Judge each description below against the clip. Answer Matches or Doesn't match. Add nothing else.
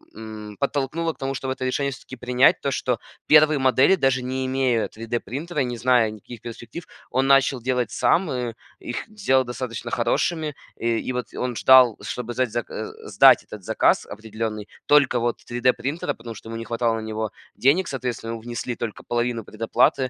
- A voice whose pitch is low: Matches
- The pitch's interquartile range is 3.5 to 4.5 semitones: Doesn't match